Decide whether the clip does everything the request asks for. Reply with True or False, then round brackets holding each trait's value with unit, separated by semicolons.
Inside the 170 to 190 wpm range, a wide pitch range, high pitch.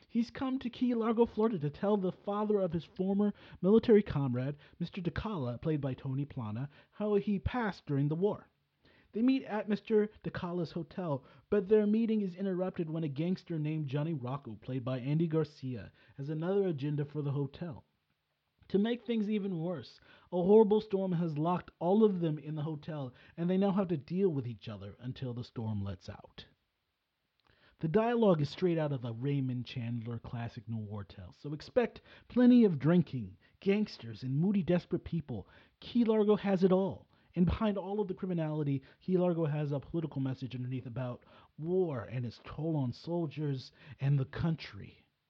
False (180 wpm; 7.0 semitones; 160 Hz)